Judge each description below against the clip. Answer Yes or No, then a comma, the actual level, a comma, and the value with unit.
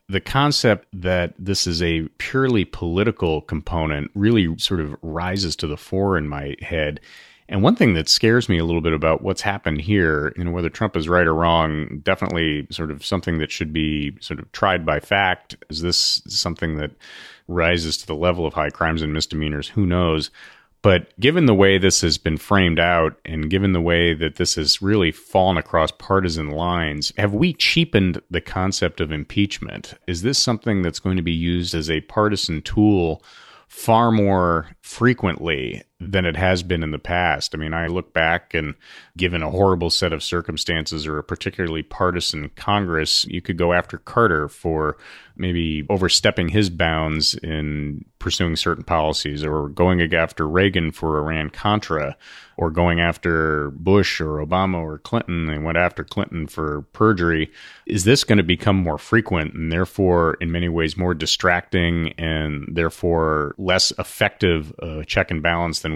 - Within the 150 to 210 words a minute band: Yes, average, 175 wpm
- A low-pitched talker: Yes, very low, 85 Hz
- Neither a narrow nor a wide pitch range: Yes, average, 3.3 semitones